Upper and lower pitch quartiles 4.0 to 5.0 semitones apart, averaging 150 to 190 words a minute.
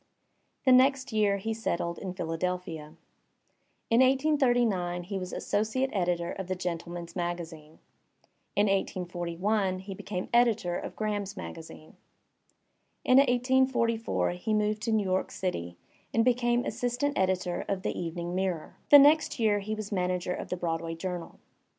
No: average, 4.6 semitones; average, 140 wpm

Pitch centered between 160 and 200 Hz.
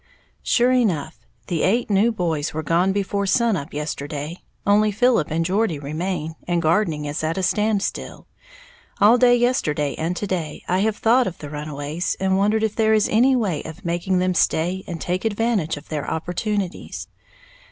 Yes: medium, 185 Hz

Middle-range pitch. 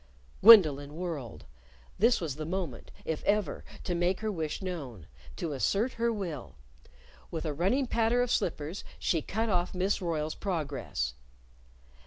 Yes: medium, 175 Hz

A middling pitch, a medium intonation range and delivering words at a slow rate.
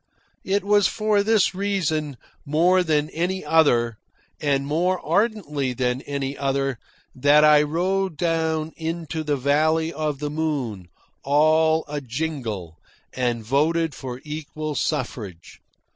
Yes: medium, 150 Hz; average, 3.2 semitones; slow, 125 wpm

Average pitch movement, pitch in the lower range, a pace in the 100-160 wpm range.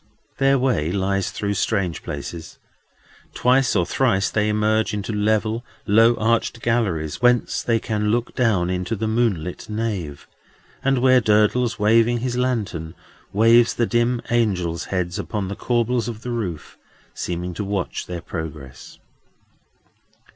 Yes: average, 4.2 semitones; low, 110 Hz; average, 140 wpm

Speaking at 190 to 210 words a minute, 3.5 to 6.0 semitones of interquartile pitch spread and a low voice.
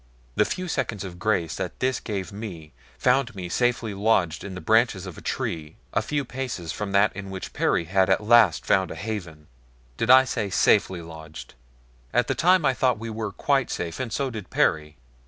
Yes: average, 200 wpm; wide, 5.6 semitones; low, 100 Hz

